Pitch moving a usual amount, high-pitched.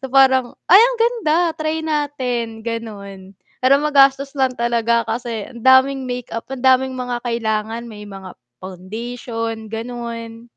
Yes: average, 3.0 semitones; high, 240 Hz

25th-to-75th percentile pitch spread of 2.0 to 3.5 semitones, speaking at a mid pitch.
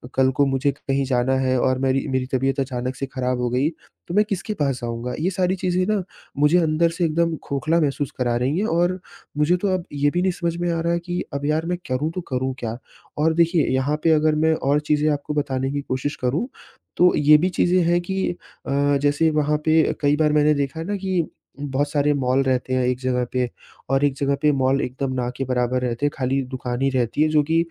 No: average, 3.9 semitones; medium, 145 Hz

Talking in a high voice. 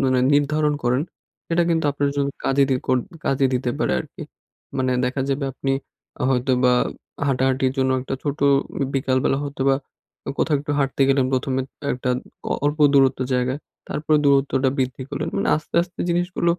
No: low, 135 Hz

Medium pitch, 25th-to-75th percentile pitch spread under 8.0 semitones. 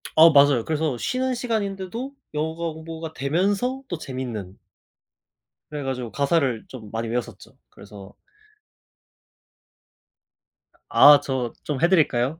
Yes: medium, 150 Hz; average, 5.3 semitones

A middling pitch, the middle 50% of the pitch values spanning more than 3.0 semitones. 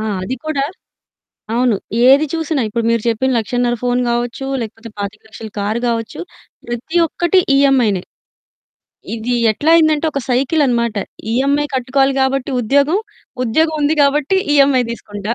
No: very high, 255 Hz; average, 3.6 semitones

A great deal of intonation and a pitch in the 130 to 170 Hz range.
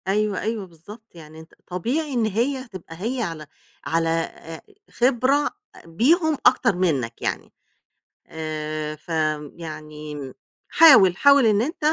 No: wide, 7.3 semitones; medium, 180 Hz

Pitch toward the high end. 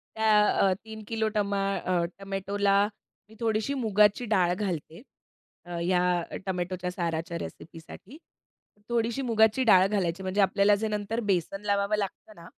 Yes: high, 200 Hz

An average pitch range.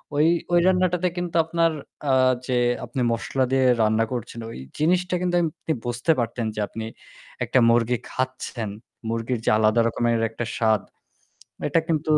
No: wide, 6.2 semitones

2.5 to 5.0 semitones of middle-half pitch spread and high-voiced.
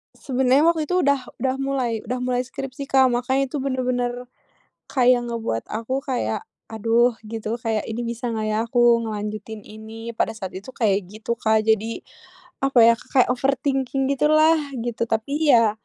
Yes: average, 3.2 semitones; high, 240 Hz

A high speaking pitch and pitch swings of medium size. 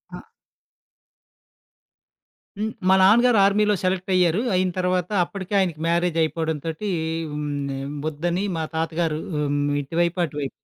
No: medium, 175 Hz; average, 3.0 semitones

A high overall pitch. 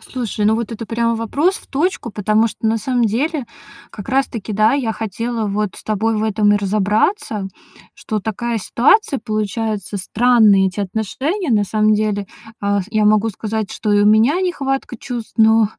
Yes: high, 220 Hz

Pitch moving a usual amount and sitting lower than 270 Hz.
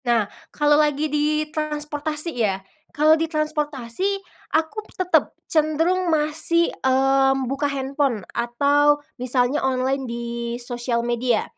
No: average, 3.3 semitones; very high, 290 Hz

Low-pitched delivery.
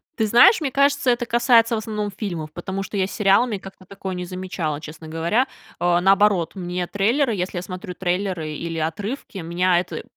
No: high, 190 Hz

